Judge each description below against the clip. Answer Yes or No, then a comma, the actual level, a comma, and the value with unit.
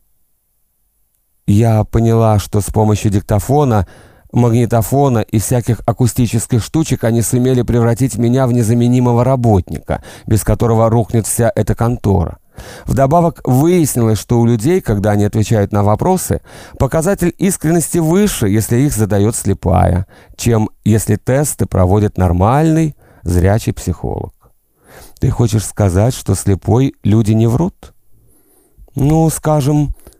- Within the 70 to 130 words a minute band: Yes, average, 115 wpm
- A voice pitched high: No, low, 115 Hz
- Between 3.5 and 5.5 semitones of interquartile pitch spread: Yes, average, 3.9 semitones